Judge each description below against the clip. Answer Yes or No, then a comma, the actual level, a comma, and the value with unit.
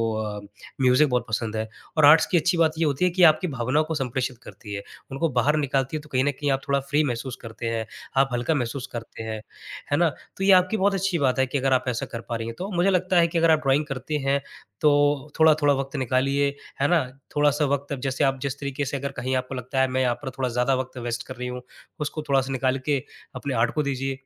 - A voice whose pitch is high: No, low, 135 Hz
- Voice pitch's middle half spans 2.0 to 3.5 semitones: Yes, average, 3.1 semitones